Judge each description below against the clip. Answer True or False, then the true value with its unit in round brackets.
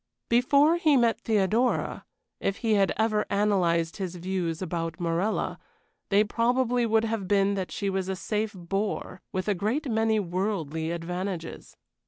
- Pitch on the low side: False (200 Hz)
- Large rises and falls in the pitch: False (3.7 semitones)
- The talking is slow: False (150 wpm)